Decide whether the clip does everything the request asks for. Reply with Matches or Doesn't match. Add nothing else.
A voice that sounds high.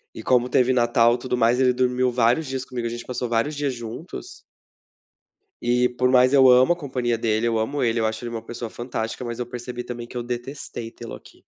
Doesn't match